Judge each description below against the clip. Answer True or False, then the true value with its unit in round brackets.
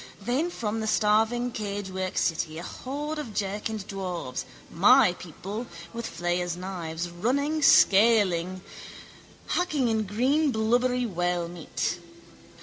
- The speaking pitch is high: True (210 Hz)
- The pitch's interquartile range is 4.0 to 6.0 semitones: True (5.4 semitones)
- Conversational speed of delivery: False (110 wpm)